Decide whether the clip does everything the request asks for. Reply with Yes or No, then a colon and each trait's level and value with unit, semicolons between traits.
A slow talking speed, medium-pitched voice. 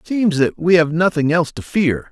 No: fast, 255 wpm; medium, 160 Hz